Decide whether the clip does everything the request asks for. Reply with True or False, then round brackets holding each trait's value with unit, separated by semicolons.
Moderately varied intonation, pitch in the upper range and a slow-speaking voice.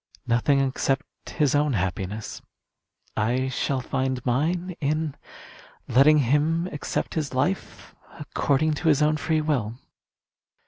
False (3.1 semitones; 140 Hz; 120 wpm)